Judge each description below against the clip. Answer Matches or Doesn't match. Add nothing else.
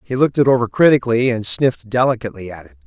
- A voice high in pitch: Doesn't match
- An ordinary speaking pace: Doesn't match